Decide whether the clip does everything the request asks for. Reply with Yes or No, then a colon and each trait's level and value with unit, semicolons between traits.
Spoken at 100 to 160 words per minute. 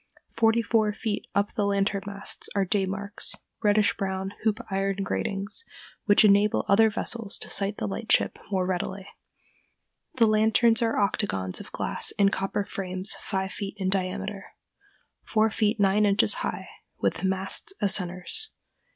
Yes: average, 150 wpm